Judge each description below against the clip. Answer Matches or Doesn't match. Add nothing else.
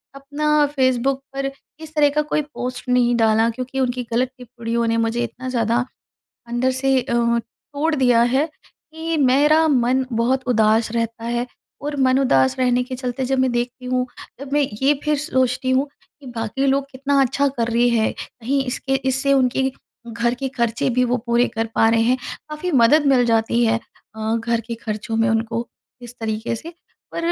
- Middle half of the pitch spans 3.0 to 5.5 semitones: Doesn't match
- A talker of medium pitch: Doesn't match